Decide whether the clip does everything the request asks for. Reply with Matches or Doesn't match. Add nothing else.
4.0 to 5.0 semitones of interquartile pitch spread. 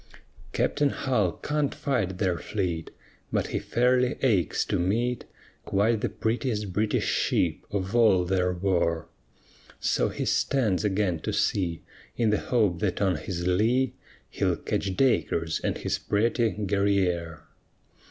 Matches